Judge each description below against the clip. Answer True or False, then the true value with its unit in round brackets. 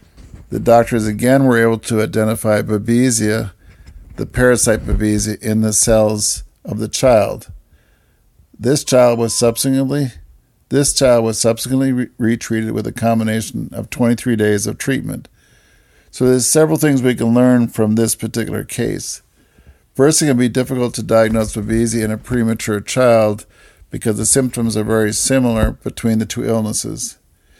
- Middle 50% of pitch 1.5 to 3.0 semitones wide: True (2.5 semitones)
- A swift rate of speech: False (145 wpm)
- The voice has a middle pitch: False (115 Hz)